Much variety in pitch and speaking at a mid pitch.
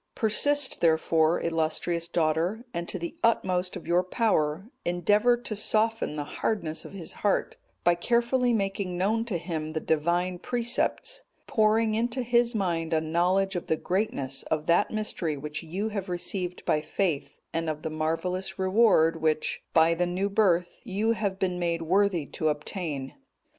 No: average, 4.7 semitones; medium, 180 Hz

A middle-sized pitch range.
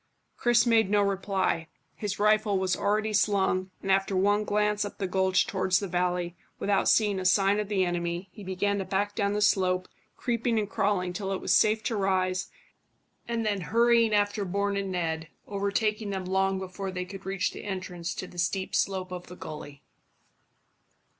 No: narrow, 2.0 semitones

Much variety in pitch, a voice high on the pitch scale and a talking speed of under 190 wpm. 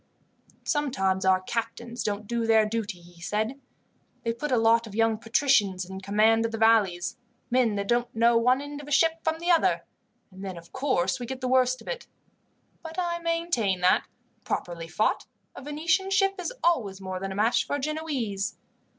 No: wide, 6.4 semitones; high, 230 Hz; average, 195 wpm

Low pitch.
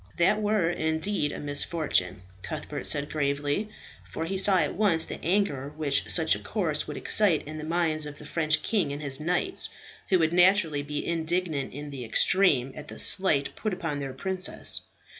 No: medium, 160 Hz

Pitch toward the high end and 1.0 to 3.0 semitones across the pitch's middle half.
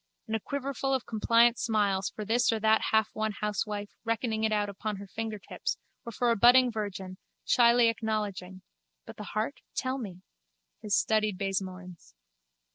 Yes: high, 215 Hz; narrow, 2.5 semitones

